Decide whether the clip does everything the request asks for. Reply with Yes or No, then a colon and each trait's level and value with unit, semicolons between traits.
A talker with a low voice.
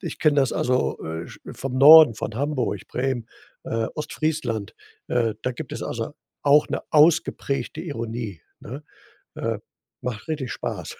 Yes: low, 130 Hz